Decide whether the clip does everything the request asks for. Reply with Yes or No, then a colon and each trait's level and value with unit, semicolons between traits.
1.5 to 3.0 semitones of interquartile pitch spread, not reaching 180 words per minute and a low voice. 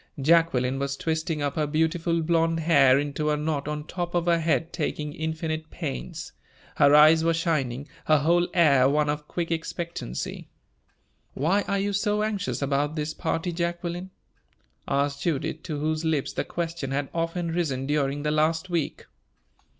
No: narrow, 2.6 semitones; average, 160 wpm; medium, 160 Hz